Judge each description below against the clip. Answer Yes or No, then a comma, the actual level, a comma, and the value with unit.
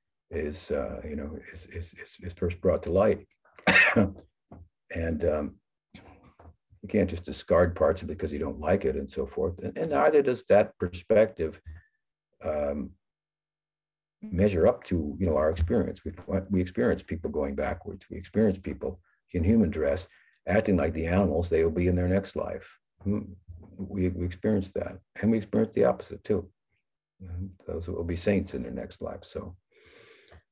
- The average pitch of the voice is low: Yes, very low, 95 Hz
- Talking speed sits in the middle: Yes, average, 170 wpm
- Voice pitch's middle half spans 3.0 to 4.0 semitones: Yes, average, 3.3 semitones